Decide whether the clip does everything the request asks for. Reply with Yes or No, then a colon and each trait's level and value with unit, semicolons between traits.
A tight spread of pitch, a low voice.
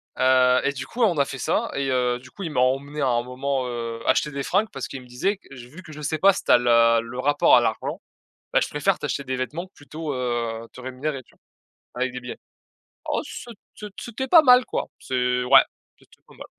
No: average, 3.3 semitones; low, 130 Hz